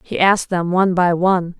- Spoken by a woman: Yes, female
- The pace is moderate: No, fast, 225 wpm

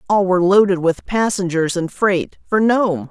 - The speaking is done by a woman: Yes, female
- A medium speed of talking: Yes, average, 175 wpm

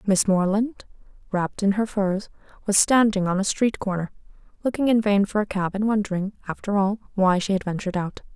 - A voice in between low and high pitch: No, high, 200 Hz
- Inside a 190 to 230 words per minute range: Yes, average, 195 wpm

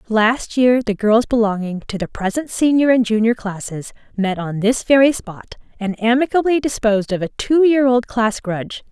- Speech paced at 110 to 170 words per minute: No, average, 180 wpm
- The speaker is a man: No, female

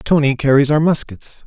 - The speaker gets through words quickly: No, average, 165 wpm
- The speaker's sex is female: No, male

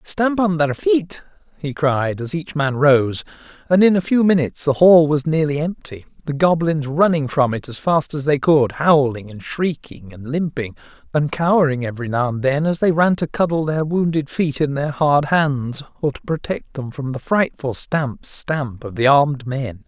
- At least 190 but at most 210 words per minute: Yes, average, 200 wpm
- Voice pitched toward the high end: No, medium, 145 Hz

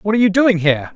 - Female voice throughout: No, male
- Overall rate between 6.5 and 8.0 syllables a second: Yes, 7.7 syllables/s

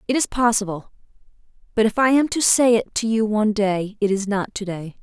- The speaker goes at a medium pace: No, fast, 225 wpm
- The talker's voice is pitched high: Yes, high, 215 Hz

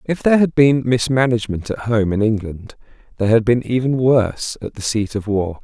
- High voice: No, low, 115 Hz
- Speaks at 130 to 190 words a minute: No, average, 200 wpm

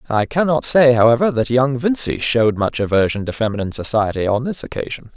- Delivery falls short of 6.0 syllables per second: No, 6.1 syllables/s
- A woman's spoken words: No, male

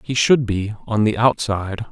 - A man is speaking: Yes, male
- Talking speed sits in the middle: Yes, average, 190 wpm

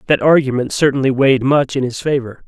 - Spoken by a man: Yes, male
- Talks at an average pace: Yes, average, 195 wpm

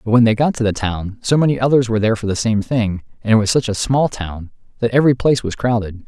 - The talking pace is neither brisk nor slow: No, fast, 275 wpm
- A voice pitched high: No, low, 115 Hz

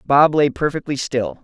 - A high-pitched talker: No, medium, 140 Hz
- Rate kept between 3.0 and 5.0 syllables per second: Yes, 4.5 syllables/s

